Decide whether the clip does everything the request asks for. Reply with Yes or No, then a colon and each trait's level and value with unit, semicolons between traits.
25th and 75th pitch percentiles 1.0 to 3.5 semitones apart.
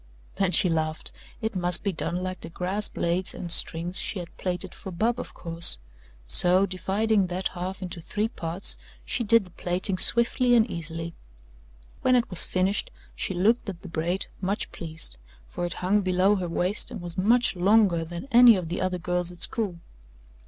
Yes: average, 2.9 semitones